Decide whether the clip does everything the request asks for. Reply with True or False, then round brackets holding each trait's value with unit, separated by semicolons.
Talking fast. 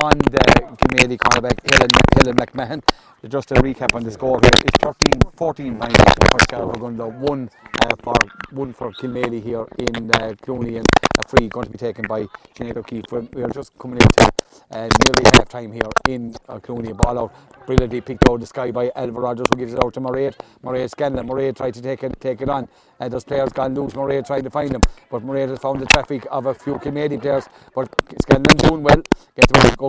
True (215 wpm)